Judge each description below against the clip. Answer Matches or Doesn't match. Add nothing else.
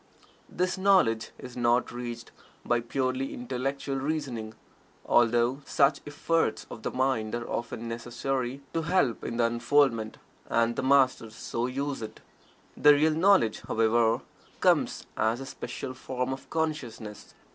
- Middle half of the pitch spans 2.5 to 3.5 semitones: Matches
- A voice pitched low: Matches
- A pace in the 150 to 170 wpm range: Doesn't match